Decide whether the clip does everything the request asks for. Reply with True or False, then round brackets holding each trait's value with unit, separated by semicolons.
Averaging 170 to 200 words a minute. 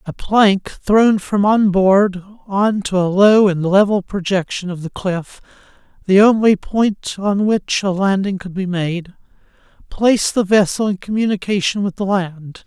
False (160 wpm)